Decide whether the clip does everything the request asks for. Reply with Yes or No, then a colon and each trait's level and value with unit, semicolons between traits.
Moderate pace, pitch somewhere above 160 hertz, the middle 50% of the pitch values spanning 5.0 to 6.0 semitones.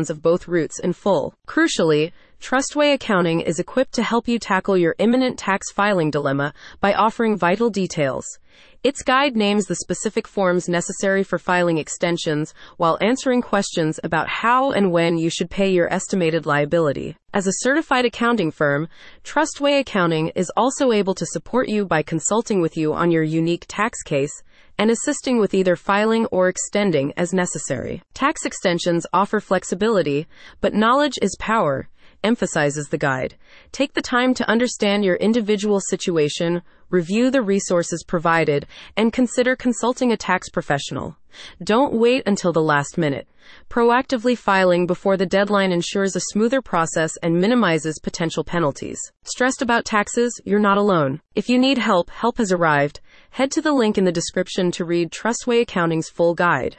Yes: average, 160 wpm; high, 190 Hz; wide, 5.6 semitones